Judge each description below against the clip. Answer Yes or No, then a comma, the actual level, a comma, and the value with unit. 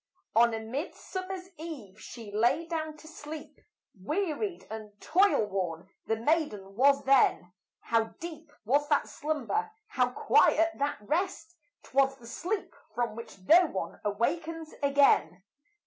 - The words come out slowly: Yes, slow, 130 wpm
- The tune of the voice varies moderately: No, wide, 6.8 semitones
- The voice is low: No, very high, 280 Hz